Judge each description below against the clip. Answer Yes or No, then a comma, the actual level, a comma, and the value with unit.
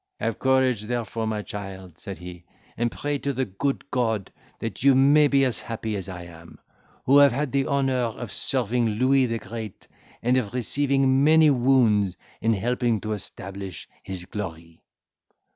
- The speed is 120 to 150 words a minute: No, average, 165 wpm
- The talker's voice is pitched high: No, low, 115 Hz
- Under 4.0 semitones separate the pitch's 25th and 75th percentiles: No, average, 4.9 semitones